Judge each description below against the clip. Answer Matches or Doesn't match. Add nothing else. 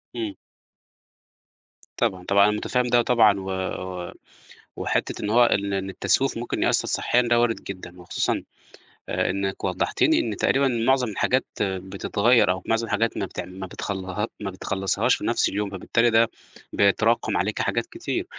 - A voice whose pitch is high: Doesn't match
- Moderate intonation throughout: Matches